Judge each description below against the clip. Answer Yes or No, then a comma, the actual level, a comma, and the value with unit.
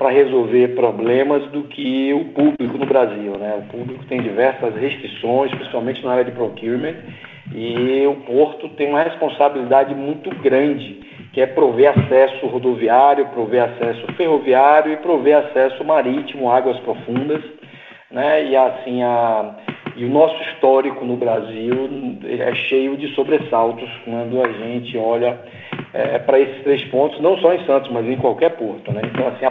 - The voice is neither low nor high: No, low, 130 Hz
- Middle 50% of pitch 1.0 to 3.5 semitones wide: Yes, average, 3.0 semitones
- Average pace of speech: Yes, average, 155 wpm